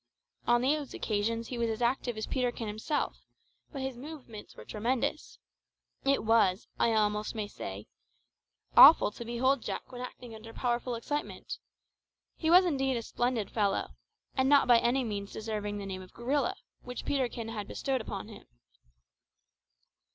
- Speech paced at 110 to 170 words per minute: Yes, average, 160 wpm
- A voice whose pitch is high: Yes, high, 235 Hz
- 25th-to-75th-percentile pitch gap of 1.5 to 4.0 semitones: Yes, average, 3.3 semitones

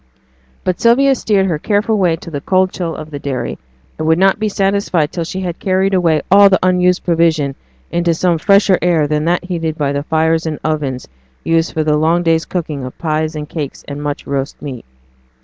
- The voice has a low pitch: No, medium, 165 Hz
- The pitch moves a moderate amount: Yes, average, 3.4 semitones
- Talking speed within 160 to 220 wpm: Yes, fast, 205 wpm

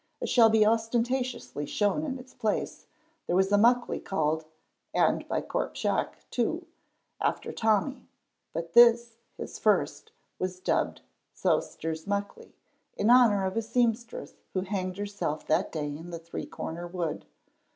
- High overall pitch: Yes, high, 205 Hz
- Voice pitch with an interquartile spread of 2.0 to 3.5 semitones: No, average, 5.3 semitones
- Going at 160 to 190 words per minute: No, average, 145 wpm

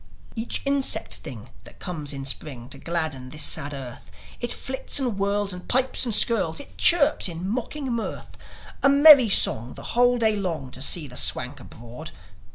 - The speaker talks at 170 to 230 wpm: Yes, average, 175 wpm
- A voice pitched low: No, medium, 180 Hz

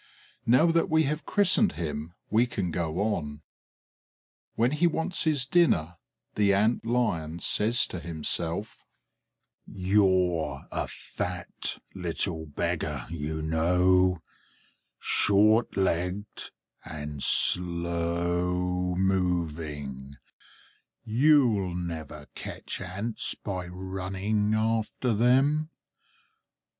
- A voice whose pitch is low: Yes, very low, 90 Hz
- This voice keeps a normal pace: No, slow, 90 wpm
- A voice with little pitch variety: No, average, 4.7 semitones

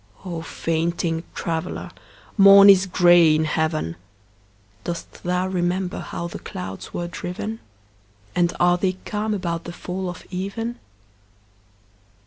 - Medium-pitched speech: Yes, medium, 175 Hz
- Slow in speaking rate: Yes, slow, 120 wpm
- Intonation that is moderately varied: No, narrow, 2.2 semitones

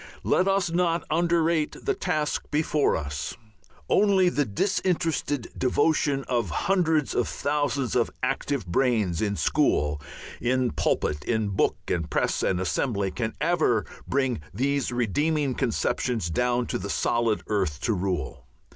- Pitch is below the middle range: Yes, low, 125 Hz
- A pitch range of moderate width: No, wide, 7.0 semitones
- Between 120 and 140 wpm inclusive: Yes, slow, 135 wpm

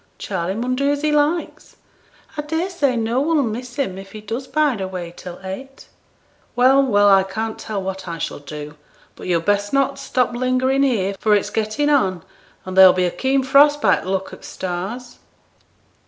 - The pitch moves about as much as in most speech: No, wide, 6.3 semitones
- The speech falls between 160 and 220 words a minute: Yes, average, 190 wpm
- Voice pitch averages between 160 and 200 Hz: No, high, 230 Hz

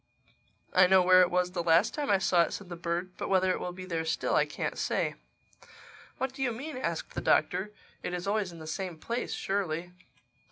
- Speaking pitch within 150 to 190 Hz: Yes, medium, 185 Hz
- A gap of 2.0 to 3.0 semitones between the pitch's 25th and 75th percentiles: Yes, narrow, 2.6 semitones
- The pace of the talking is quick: Yes, fast, 225 wpm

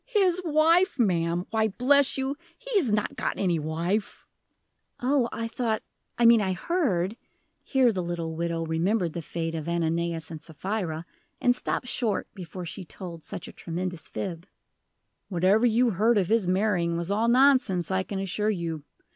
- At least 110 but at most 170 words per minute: Yes, average, 165 wpm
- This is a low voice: No, high, 190 Hz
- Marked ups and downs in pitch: Yes, wide, 5.7 semitones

